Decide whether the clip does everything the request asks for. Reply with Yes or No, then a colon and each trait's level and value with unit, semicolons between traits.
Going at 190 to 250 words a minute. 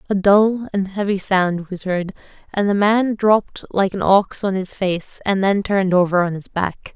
Yes: fast, 205 wpm